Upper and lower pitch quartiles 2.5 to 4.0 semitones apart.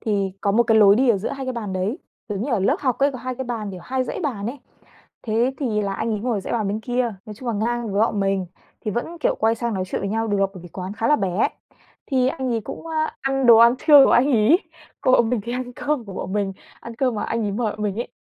Yes: average, 3.7 semitones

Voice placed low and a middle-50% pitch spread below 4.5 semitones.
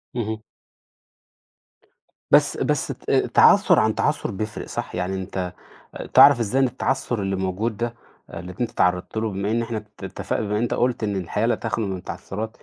Yes: low, 105 Hz; average, 3.4 semitones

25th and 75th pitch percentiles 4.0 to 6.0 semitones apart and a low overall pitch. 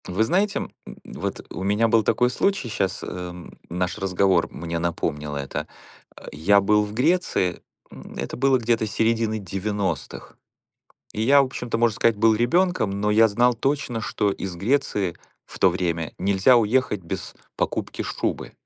Yes: average, 4.4 semitones; low, 105 Hz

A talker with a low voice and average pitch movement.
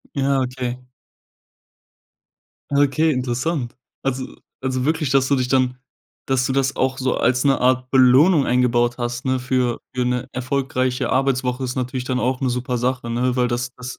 No: low, 130 Hz; narrow, 1.1 semitones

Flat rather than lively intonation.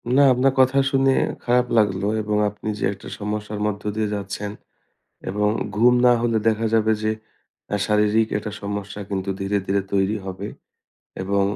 Yes: narrow, 2.0 semitones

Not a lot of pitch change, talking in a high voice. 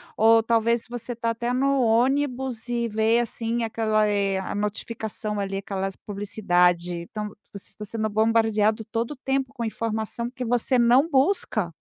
Yes: narrow, 2.3 semitones; high, 225 Hz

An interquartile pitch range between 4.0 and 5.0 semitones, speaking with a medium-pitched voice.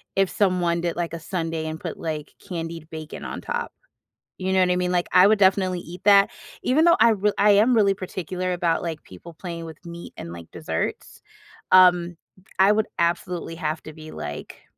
No: narrow, 2.5 semitones; medium, 175 Hz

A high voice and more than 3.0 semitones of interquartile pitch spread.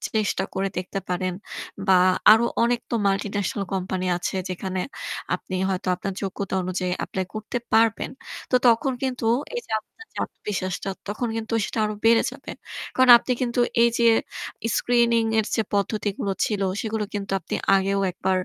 Yes: high, 205 Hz; average, 3.4 semitones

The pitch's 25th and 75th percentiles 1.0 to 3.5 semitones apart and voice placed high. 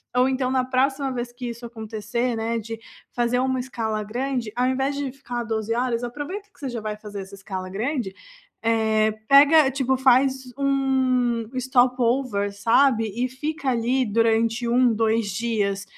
Yes: average, 2.7 semitones; high, 245 Hz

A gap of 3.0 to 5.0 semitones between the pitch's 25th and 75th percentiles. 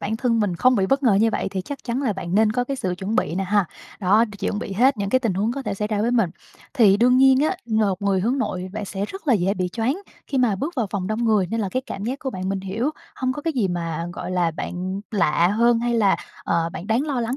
Yes: average, 4.4 semitones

